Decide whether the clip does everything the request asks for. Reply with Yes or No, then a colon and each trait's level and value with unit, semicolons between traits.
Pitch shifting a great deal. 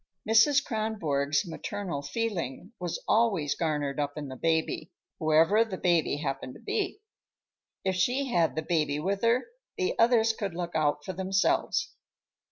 Yes: wide, 6.6 semitones